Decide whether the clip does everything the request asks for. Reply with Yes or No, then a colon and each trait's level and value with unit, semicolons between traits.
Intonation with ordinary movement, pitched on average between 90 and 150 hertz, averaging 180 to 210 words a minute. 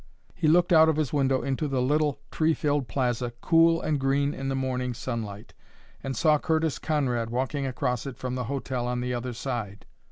Yes: average, 3.2 semitones; low, 135 Hz; average, 195 wpm